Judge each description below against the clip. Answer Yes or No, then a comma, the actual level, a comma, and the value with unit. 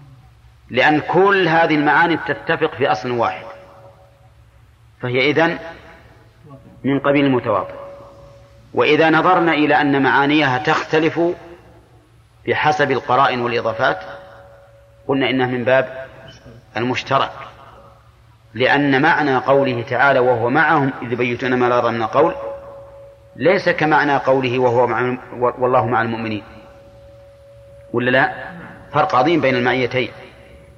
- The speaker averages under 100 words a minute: No, average, 105 wpm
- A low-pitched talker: Yes, low, 125 Hz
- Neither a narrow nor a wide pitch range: Yes, average, 3.7 semitones